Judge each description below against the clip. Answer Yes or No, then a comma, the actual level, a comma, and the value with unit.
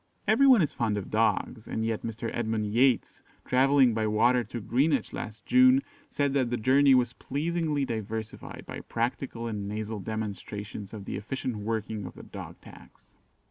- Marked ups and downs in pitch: No, average, 3.9 semitones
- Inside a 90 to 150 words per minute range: No, average, 170 wpm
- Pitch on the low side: Yes, low, 115 Hz